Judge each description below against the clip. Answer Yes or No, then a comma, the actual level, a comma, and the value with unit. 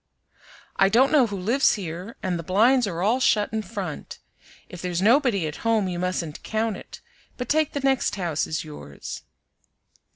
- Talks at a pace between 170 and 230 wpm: Yes, average, 175 wpm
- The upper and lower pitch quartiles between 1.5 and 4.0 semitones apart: No, average, 5.2 semitones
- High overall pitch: Yes, high, 200 Hz